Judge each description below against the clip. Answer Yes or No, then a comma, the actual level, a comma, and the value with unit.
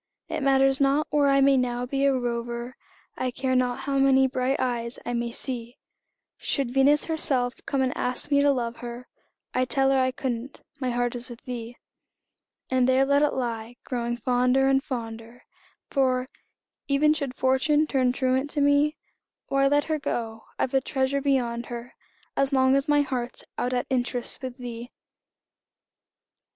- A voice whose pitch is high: Yes, very high, 260 Hz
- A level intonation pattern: Yes, narrow, 2.1 semitones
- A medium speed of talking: Yes, average, 170 wpm